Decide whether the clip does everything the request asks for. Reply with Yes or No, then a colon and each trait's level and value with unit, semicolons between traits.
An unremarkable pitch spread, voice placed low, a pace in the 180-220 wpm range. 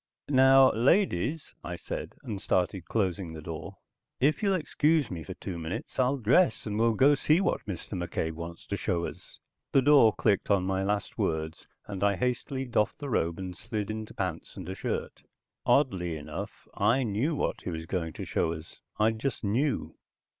No: wide, 7.2 semitones; low, 105 Hz; average, 185 wpm